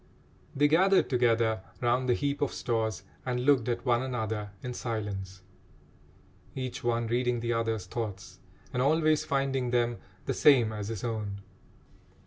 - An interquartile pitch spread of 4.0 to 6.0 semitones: No, average, 2.8 semitones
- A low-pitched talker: Yes, low, 120 Hz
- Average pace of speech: Yes, average, 145 wpm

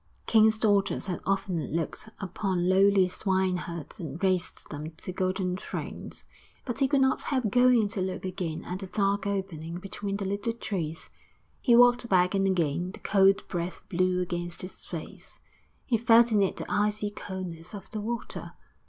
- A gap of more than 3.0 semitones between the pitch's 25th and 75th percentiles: No, average, 2.7 semitones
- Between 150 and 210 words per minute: Yes, average, 170 wpm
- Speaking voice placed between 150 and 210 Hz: Yes, high, 190 Hz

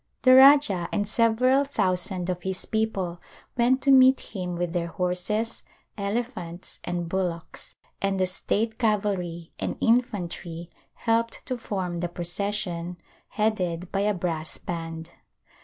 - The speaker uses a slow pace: Yes, slow, 130 wpm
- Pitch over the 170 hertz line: Yes, high, 190 Hz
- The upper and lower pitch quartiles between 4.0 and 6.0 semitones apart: Yes, average, 4.4 semitones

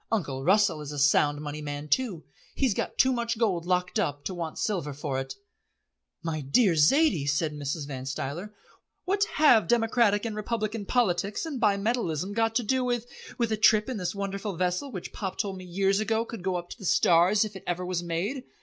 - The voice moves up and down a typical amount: No, wide, 5.7 semitones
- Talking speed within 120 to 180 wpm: No, fast, 205 wpm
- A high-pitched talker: Yes, high, 195 Hz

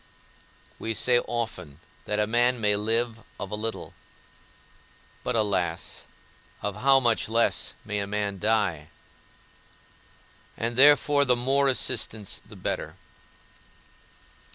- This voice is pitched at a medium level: No, low, 110 Hz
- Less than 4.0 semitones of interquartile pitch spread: Yes, average, 2.9 semitones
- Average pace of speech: No, slow, 115 wpm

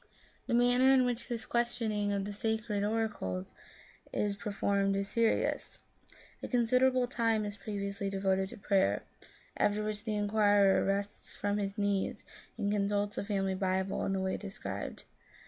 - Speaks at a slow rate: No, average, 155 wpm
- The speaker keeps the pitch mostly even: Yes, narrow, 2.1 semitones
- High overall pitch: Yes, high, 205 Hz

